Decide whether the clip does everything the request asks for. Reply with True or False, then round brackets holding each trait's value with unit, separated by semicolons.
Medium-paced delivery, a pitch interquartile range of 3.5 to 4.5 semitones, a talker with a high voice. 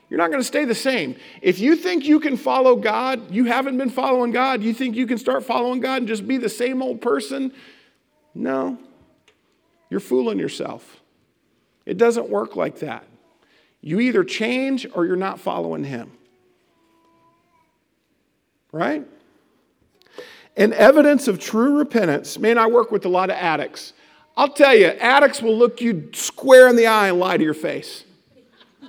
True (165 wpm; 3.9 semitones; 255 Hz)